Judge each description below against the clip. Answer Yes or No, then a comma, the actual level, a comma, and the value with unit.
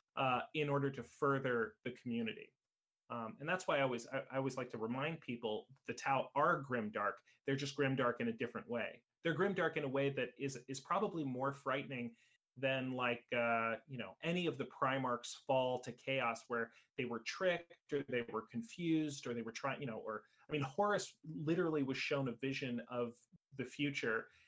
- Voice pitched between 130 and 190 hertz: Yes, low, 135 Hz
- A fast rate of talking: No, average, 195 wpm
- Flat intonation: No, average, 3.6 semitones